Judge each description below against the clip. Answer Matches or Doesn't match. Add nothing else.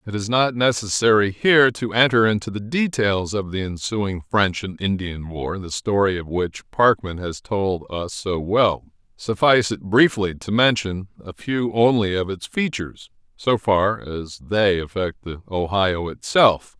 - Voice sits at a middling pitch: Doesn't match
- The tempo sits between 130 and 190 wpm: Matches